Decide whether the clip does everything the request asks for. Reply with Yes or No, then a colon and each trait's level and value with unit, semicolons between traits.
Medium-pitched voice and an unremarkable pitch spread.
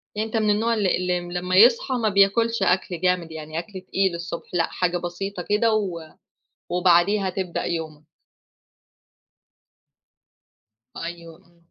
Yes: medium, 180 Hz; average, 3.2 semitones